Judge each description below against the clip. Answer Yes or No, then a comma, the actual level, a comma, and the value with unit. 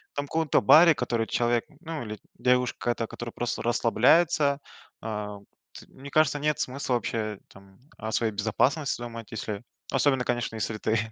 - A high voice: No, low, 120 Hz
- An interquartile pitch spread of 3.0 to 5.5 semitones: Yes, average, 4.2 semitones